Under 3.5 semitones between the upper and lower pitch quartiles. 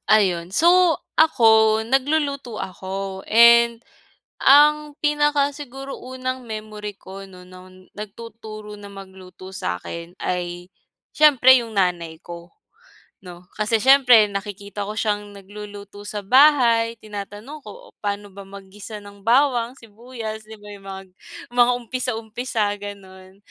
No: average, 4.0 semitones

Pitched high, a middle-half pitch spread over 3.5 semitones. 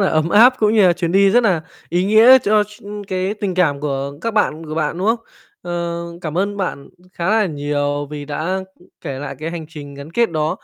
No: medium, 175 Hz; average, 5.1 semitones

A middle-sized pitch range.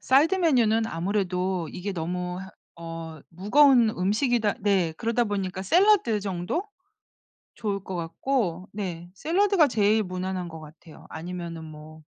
Yes: average, 4.6 semitones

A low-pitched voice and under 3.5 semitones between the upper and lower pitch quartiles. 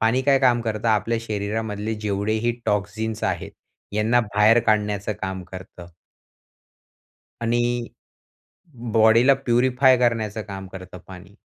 Yes: low, 110 Hz; narrow, 2.5 semitones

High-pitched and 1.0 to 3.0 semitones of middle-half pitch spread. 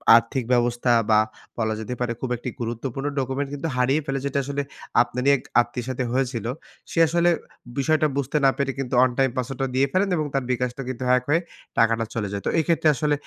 No: low, 130 Hz; narrow, 2.5 semitones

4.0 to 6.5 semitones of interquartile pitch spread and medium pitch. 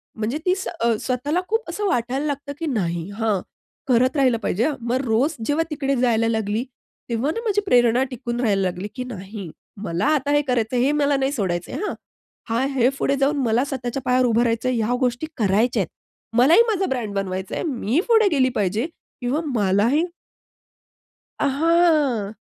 No: average, 4.5 semitones; very high, 250 Hz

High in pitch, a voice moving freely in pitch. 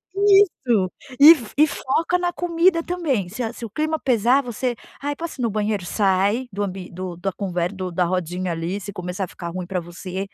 Yes: high, 205 Hz; wide, 7.6 semitones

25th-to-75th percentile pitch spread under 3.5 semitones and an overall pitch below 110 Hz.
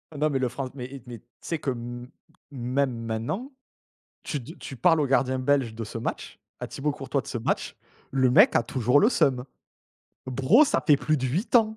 No: average, 3.0 semitones; low, 130 Hz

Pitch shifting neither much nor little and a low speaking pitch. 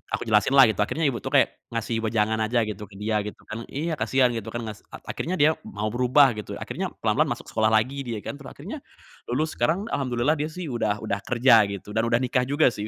Yes: average, 4.2 semitones; low, 120 Hz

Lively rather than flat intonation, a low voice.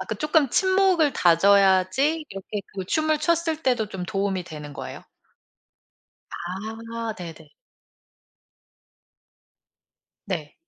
No: wide, 8.6 semitones; high, 210 Hz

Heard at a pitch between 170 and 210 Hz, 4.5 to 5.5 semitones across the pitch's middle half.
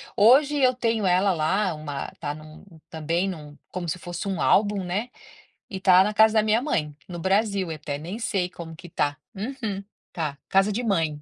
Yes: medium, 185 Hz; average, 4.8 semitones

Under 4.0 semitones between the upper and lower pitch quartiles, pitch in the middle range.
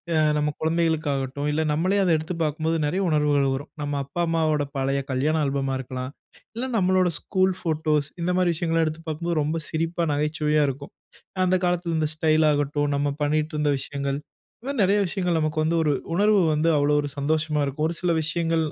Yes: narrow, 2.5 semitones; medium, 155 Hz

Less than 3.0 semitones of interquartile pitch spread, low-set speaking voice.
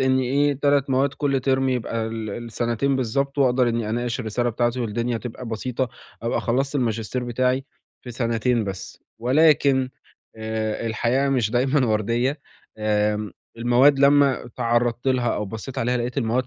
Yes: narrow, 2.6 semitones; low, 120 Hz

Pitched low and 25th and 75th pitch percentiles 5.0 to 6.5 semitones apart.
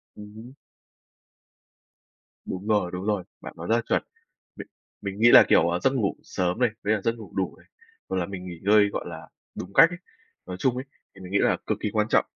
No: low, 100 Hz; average, 3.3 semitones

